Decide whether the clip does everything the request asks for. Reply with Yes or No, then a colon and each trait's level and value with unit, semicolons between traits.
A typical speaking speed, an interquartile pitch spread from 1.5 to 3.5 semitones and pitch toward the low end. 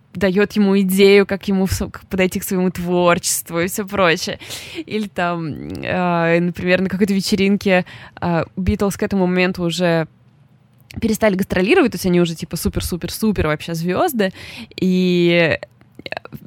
No: average, 140 wpm; narrow, 2.4 semitones; medium, 185 Hz